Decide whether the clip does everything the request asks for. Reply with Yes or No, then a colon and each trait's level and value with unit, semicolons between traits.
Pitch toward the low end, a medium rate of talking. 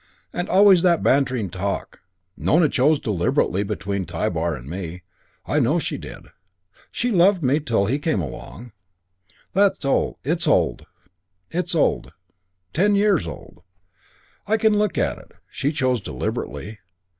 No: low, 130 Hz; slow, 125 wpm